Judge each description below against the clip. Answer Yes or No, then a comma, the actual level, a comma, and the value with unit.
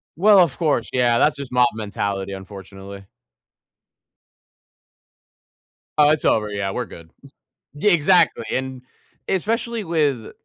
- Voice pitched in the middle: No, low, 125 Hz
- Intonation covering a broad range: Yes, wide, 7.7 semitones